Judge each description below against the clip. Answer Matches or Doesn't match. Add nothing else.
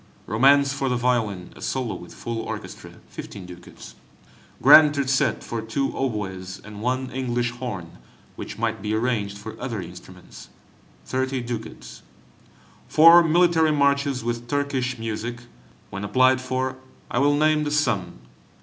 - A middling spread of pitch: Matches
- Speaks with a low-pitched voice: Matches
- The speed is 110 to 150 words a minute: Matches